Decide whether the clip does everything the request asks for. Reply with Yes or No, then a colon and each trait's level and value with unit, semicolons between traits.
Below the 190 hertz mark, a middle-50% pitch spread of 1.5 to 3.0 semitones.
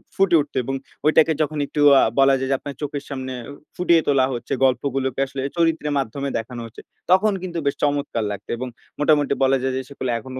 Yes: medium, 140 Hz; narrow, 2.4 semitones